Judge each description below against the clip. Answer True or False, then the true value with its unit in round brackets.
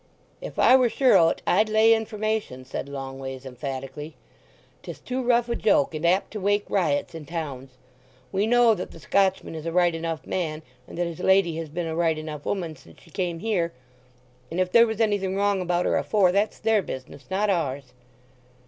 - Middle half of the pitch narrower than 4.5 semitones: False (5.0 semitones)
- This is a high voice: False (175 Hz)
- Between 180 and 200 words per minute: True (195 wpm)